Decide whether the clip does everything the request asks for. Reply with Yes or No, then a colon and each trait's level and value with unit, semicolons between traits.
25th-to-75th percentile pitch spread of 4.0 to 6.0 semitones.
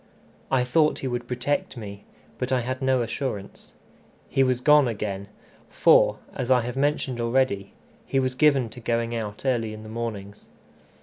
No: average, 2.9 semitones